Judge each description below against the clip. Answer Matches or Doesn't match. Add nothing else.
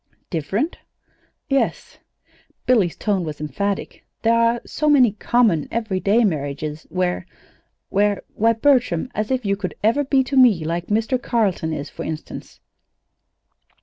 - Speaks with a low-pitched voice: Doesn't match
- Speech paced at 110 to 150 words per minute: Matches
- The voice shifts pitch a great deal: Matches